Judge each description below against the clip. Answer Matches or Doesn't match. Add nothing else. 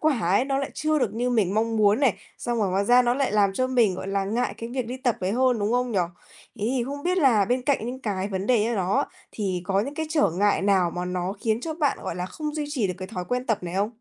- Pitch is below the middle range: Doesn't match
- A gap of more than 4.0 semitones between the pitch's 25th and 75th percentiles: Matches